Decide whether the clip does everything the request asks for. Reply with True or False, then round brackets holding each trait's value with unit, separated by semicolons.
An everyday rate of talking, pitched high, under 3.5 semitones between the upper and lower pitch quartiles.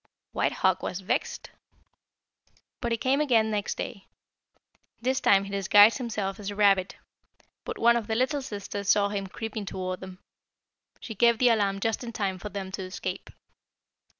True (170 wpm; 205 Hz; 3.0 semitones)